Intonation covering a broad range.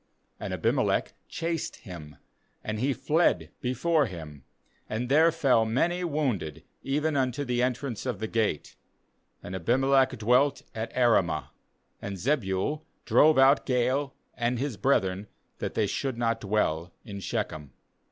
Yes: wide, 5.8 semitones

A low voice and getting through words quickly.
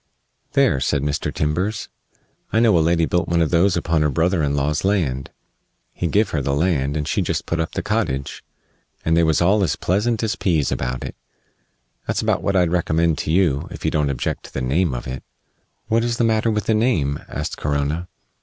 Yes: very low, 80 Hz; fast, 210 wpm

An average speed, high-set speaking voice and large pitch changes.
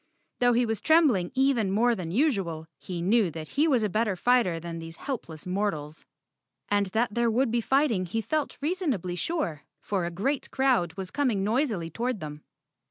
Yes: average, 180 wpm; high, 215 Hz; wide, 6.4 semitones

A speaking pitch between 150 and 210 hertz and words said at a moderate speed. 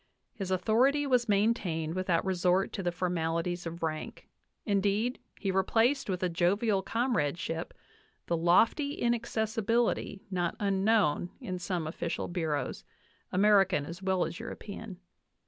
No: high, 190 Hz; slow, 125 wpm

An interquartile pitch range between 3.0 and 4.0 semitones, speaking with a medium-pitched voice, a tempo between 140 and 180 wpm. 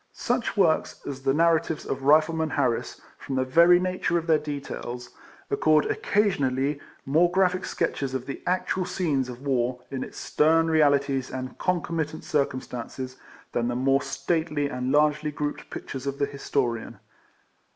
Yes: average, 3.7 semitones; medium, 145 Hz; average, 150 wpm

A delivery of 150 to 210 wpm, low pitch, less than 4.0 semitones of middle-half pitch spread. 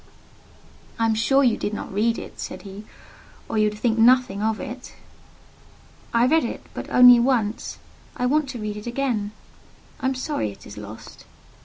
No: average, 180 wpm; high, 230 Hz; average, 3.2 semitones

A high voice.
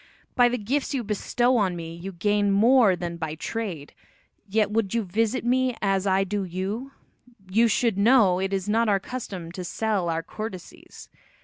Yes: high, 205 Hz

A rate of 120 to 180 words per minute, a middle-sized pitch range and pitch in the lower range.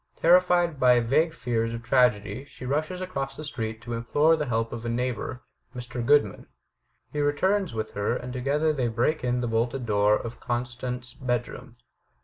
Yes: average, 175 wpm; average, 3.9 semitones; low, 125 Hz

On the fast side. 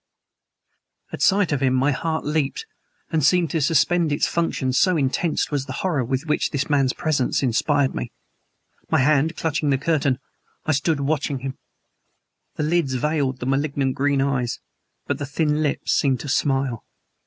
No: average, 165 wpm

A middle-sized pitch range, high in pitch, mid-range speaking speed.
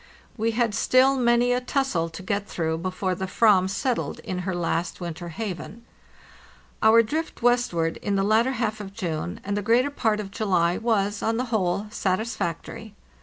Yes: average, 4.2 semitones; high, 210 Hz; average, 170 wpm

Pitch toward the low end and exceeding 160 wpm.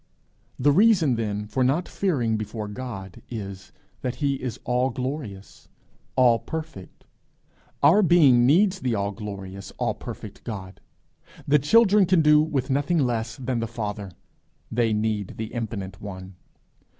No: low, 120 Hz; average, 140 wpm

